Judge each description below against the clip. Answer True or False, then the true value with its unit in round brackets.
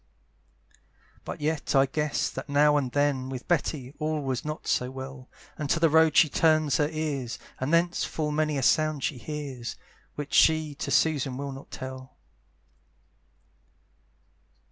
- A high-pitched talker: False (145 Hz)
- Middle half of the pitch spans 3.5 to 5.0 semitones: False (2.6 semitones)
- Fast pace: False (155 wpm)